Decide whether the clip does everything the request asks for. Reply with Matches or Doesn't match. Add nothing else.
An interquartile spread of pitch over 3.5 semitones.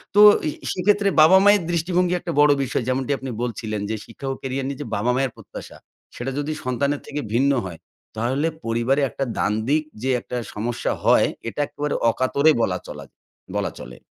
Matches